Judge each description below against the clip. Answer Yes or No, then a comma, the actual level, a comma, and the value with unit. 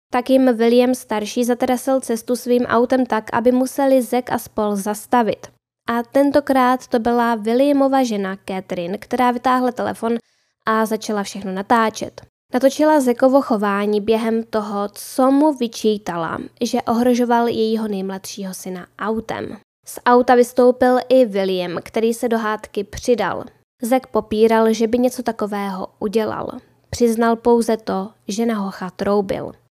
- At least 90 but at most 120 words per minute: No, average, 135 wpm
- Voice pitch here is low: No, high, 235 Hz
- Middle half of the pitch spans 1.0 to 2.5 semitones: No, average, 2.9 semitones